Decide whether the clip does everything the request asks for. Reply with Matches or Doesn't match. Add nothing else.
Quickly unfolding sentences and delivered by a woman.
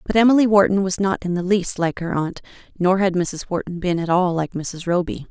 Matches